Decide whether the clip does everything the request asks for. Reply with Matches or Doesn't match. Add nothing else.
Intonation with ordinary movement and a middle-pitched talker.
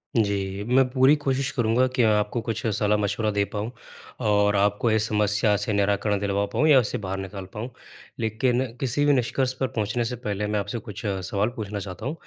Doesn't match